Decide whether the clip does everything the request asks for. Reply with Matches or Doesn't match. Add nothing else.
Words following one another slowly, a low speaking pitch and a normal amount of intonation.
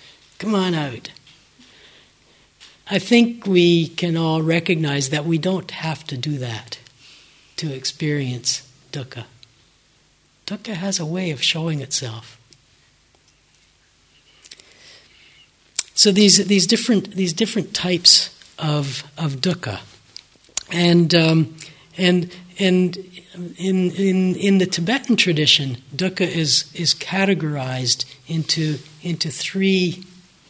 Doesn't match